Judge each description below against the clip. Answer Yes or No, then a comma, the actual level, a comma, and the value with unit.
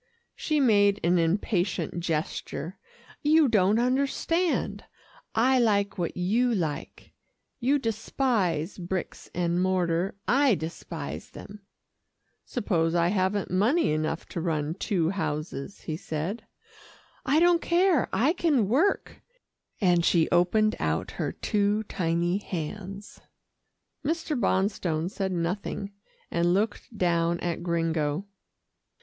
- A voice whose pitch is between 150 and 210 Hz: Yes, high, 190 Hz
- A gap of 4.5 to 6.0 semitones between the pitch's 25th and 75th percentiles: Yes, average, 5.0 semitones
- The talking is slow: Yes, slow, 115 wpm